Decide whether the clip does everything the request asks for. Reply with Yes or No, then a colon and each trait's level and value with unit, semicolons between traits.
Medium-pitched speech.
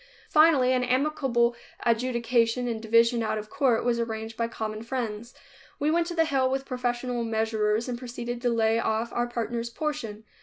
No: high, 235 Hz